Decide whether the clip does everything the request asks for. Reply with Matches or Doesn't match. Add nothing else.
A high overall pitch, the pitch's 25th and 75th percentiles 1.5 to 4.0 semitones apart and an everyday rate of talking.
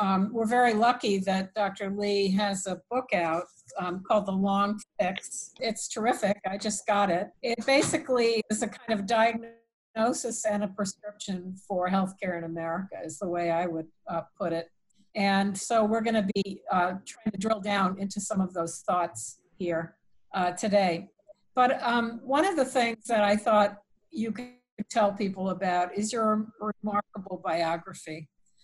Matches